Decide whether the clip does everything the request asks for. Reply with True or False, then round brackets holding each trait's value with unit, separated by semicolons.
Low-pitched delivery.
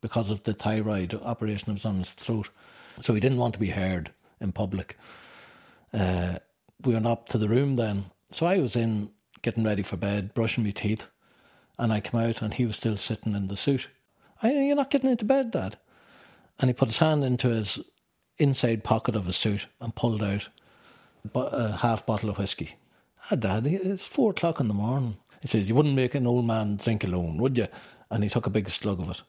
True (110 Hz)